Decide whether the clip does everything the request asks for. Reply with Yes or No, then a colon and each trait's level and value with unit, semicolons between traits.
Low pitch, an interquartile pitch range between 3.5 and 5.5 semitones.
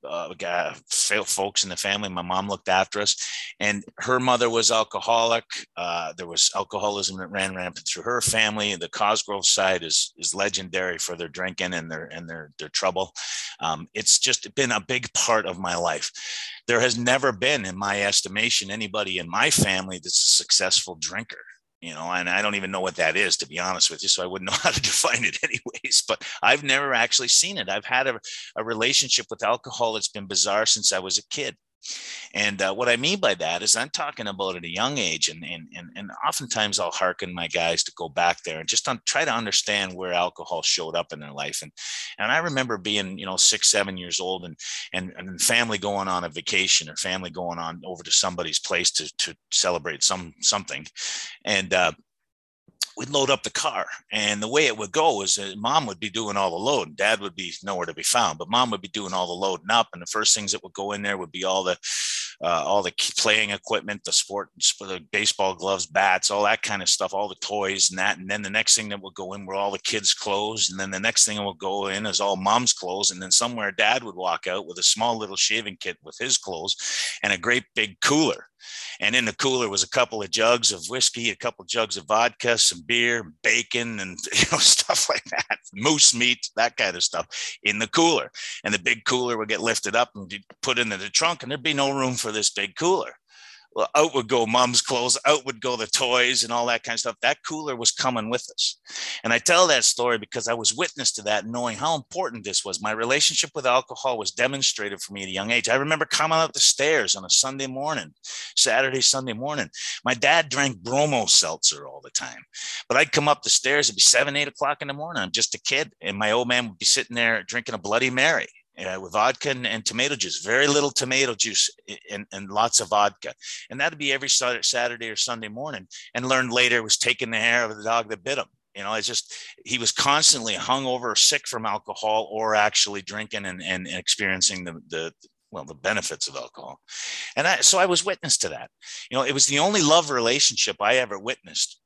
Yes: low, 110 Hz; average, 4.4 semitones